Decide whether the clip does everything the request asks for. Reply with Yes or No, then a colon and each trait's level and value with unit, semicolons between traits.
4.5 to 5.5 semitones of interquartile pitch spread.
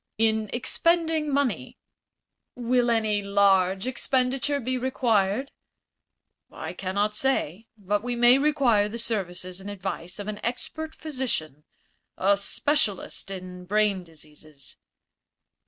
Yes: average, 5.0 semitones